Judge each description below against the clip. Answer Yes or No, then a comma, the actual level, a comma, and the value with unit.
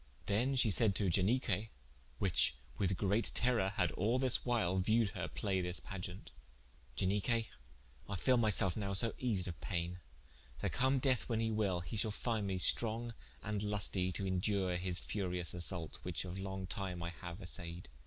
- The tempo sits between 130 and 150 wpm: No, average, 175 wpm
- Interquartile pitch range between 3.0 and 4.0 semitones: Yes, average, 3.7 semitones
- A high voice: No, low, 100 Hz